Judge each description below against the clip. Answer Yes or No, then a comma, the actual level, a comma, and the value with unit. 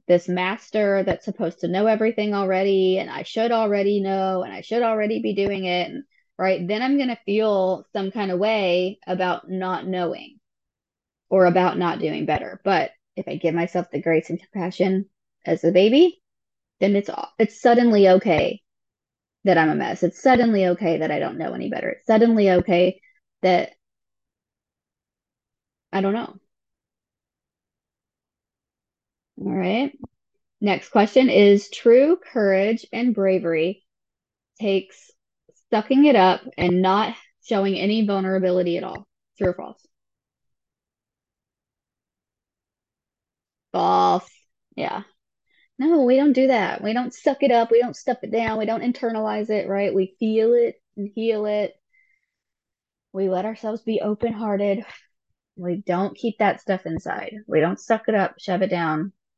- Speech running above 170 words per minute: No, average, 150 wpm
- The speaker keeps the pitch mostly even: No, average, 3.6 semitones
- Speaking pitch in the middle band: No, high, 200 Hz